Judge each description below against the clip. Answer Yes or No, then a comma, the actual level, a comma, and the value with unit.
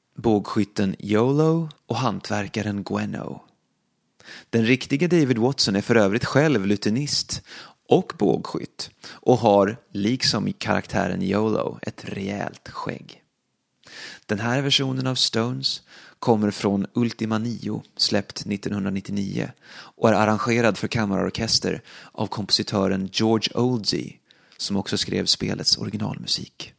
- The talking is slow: Yes, slow, 110 wpm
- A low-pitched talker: Yes, low, 110 Hz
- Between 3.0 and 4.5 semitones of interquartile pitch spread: Yes, average, 3.5 semitones